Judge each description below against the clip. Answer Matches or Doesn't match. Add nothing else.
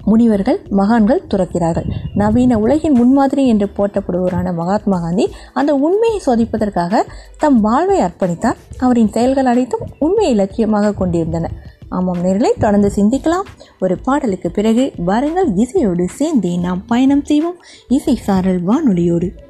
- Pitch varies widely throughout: Matches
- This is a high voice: Matches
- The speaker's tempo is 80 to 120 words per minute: Matches